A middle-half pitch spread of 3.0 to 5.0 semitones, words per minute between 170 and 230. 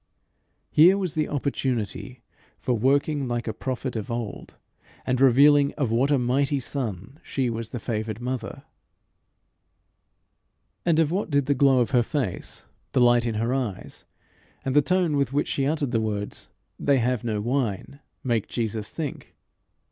No: average, 3.5 semitones; average, 160 wpm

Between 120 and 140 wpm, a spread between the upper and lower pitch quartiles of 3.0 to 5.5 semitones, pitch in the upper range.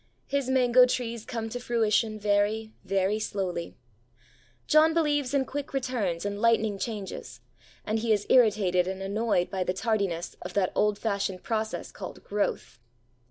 No: average, 150 wpm; average, 3.4 semitones; high, 215 Hz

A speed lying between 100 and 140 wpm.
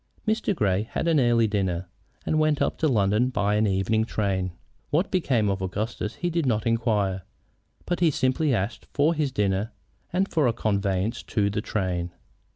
No: average, 170 wpm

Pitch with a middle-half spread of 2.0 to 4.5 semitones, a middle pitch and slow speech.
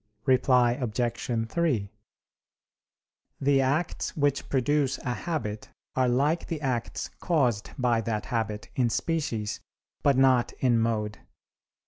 No: average, 3.7 semitones; low, 125 Hz; slow, 115 wpm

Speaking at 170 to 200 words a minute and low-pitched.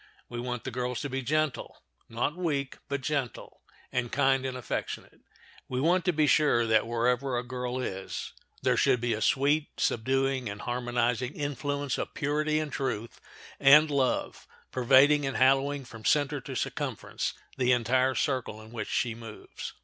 No: average, 155 wpm; low, 130 Hz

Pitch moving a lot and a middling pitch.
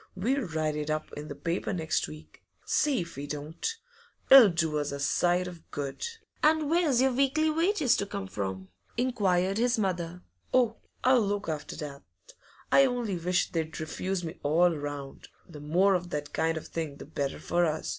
Yes: wide, 7.6 semitones; medium, 175 Hz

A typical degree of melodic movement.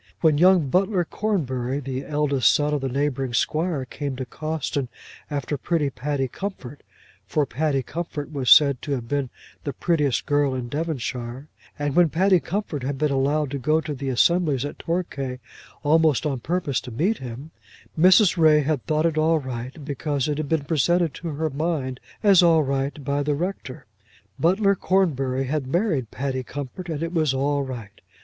Yes: average, 3.3 semitones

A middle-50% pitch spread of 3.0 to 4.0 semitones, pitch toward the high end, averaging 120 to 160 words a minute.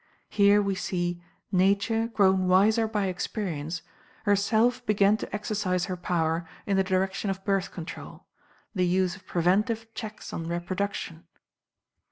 No: narrow, 2.6 semitones; high, 195 Hz; slow, 135 wpm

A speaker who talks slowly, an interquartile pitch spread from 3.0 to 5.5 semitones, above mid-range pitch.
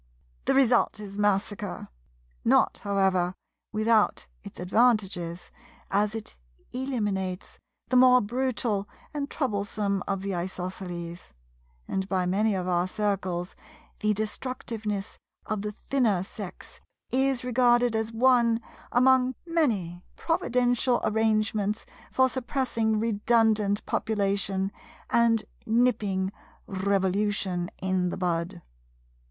Yes: slow, 100 wpm; average, 3.8 semitones; high, 210 Hz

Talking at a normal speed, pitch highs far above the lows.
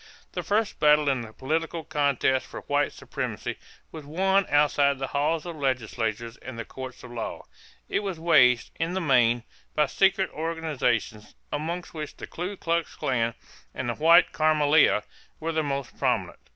No: average, 165 wpm; average, 4.3 semitones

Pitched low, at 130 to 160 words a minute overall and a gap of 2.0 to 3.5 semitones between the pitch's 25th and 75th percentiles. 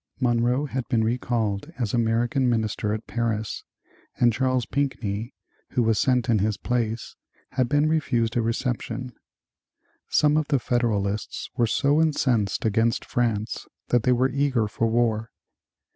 Yes: low, 120 Hz; average, 145 wpm; narrow, 2.4 semitones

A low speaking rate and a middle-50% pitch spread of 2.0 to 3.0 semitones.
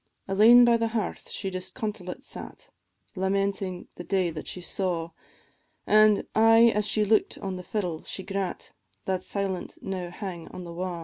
No: average, 165 wpm; average, 2.7 semitones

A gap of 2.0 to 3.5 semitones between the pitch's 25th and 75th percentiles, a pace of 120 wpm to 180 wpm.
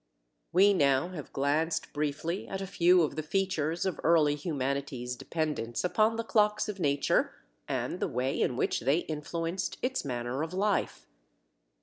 No: average, 4.8 semitones; average, 155 wpm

